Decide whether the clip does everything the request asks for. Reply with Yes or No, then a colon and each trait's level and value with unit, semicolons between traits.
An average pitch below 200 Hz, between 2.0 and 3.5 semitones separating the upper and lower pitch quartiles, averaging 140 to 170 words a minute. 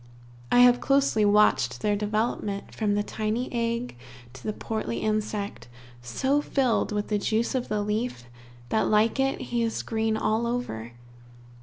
No: high, 220 Hz; narrow, 2.4 semitones; average, 155 wpm